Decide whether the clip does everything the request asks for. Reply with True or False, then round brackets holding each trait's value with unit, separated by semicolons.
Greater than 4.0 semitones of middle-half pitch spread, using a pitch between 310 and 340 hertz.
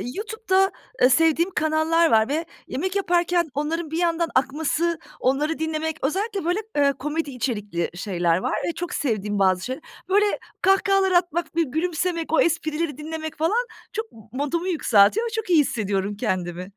True (5.2 semitones; 320 Hz)